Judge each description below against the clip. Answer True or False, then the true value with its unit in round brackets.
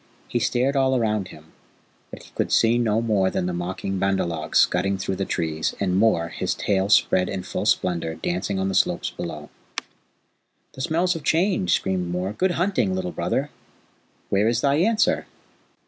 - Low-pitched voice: True (95 Hz)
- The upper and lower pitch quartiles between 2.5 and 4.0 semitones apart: False (5.1 semitones)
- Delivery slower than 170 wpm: False (180 wpm)